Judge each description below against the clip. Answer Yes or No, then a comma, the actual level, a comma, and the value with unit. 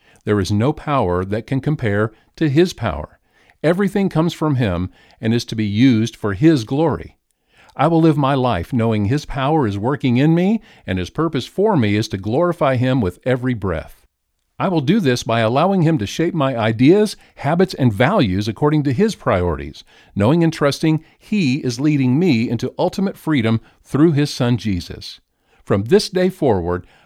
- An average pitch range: No, wide, 6.8 semitones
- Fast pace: No, average, 180 wpm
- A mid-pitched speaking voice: No, low, 130 Hz